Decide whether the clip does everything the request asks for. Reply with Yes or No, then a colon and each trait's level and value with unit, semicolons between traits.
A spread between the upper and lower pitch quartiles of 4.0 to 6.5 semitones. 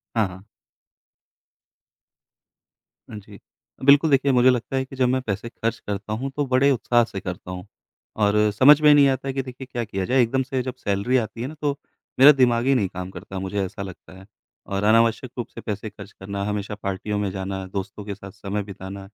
Yes: average, 4.8 semitones